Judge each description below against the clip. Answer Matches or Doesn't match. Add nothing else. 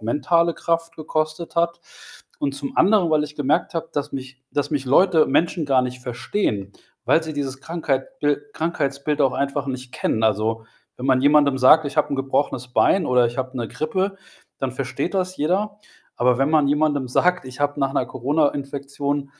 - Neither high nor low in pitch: Matches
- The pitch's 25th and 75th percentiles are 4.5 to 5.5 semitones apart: Doesn't match